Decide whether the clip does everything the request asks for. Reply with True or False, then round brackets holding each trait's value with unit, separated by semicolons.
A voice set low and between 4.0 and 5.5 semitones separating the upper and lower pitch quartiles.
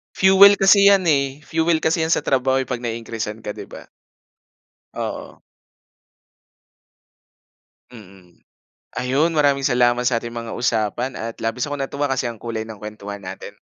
True (125 Hz; 4.4 semitones)